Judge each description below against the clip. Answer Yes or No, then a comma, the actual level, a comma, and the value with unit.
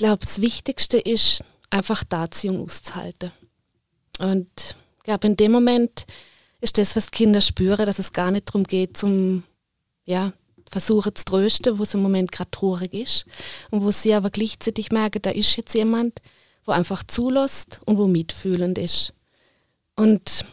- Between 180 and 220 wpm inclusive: No, average, 165 wpm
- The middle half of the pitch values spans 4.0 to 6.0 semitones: No, average, 2.8 semitones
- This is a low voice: No, high, 205 Hz